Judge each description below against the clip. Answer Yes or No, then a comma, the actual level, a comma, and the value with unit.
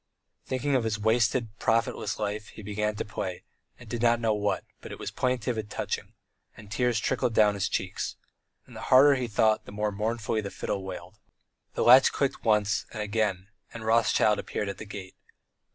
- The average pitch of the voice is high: No, low, 110 Hz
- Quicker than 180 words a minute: Yes, average, 190 wpm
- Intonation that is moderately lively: No, narrow, 2.2 semitones